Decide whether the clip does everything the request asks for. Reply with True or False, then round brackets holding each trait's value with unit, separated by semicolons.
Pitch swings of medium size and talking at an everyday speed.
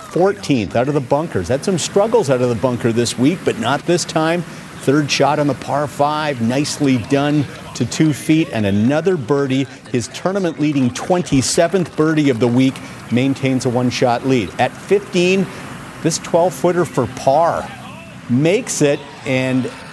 True (4.1 semitones; 165 wpm)